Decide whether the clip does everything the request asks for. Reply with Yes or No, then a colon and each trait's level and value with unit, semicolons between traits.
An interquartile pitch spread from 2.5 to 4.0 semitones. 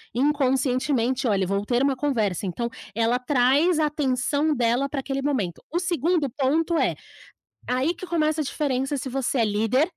Yes: average, 3.6 semitones